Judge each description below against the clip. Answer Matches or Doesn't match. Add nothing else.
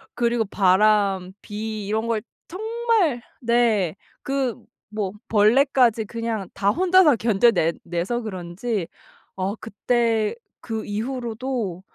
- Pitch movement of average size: Matches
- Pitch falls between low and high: Doesn't match